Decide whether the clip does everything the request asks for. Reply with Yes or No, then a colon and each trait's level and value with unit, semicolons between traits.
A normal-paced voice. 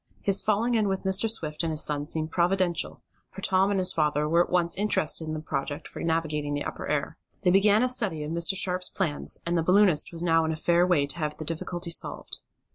No: fast, 235 wpm